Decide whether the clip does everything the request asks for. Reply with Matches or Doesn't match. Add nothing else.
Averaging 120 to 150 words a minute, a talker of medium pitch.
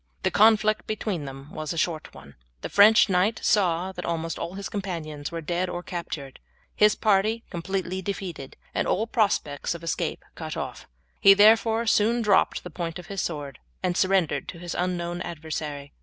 Doesn't match